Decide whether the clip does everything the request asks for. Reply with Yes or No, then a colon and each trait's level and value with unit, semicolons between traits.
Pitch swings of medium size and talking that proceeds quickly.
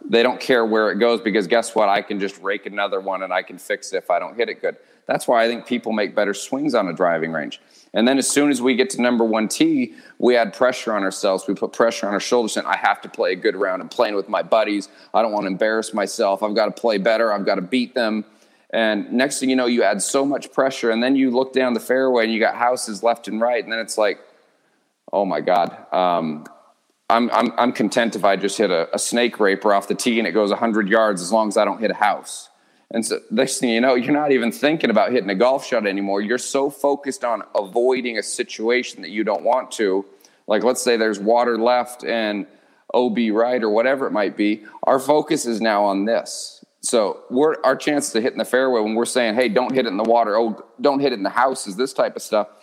Yes: average, 3.4 semitones; fast, 260 wpm